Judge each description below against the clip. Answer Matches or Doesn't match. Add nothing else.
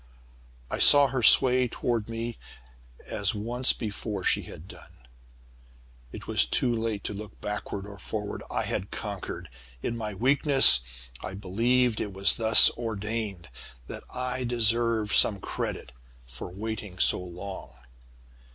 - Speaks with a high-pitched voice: Doesn't match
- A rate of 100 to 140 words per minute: Matches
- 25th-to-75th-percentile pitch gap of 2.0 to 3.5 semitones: Matches